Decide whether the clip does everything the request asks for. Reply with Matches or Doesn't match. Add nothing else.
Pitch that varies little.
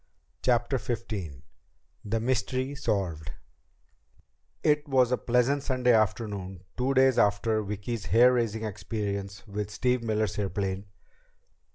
Doesn't match